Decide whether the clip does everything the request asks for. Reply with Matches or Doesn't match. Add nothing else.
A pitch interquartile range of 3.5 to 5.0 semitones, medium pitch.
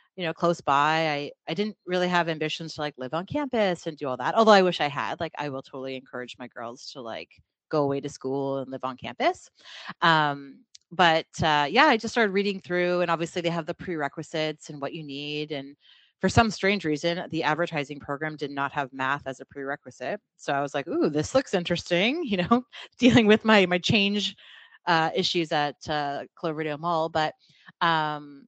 Matches